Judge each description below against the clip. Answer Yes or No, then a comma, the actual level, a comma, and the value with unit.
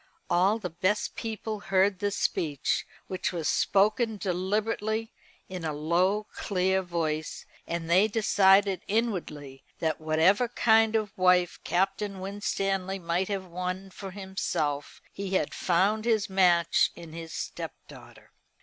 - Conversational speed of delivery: No, slow, 130 wpm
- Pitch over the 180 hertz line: Yes, high, 190 Hz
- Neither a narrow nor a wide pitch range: Yes, average, 3.0 semitones